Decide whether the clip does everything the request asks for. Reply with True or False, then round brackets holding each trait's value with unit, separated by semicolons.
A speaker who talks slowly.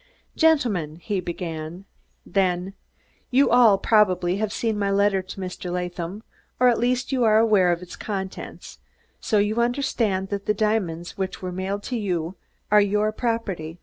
False (160 wpm)